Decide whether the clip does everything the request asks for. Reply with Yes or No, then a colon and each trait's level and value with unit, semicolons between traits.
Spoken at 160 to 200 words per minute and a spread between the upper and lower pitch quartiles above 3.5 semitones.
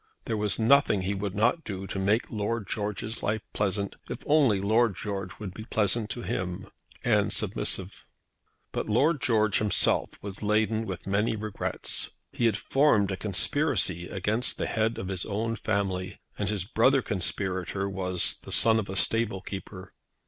No: average, 165 wpm; narrow, 2.5 semitones